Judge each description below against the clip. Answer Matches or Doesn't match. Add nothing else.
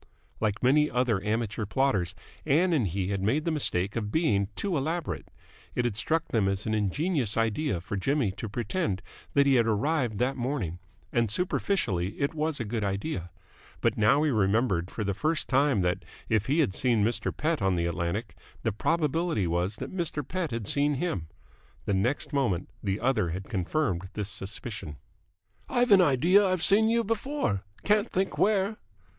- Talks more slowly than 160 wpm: Doesn't match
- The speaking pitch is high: Doesn't match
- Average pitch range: Doesn't match